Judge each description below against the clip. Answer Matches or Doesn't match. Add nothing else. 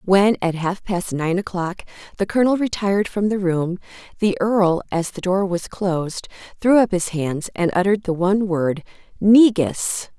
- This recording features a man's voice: Doesn't match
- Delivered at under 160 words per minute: Doesn't match